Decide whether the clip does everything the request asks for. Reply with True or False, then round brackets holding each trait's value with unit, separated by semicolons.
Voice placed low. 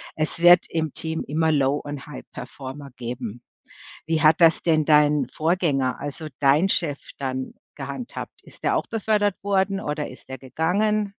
False (155 Hz)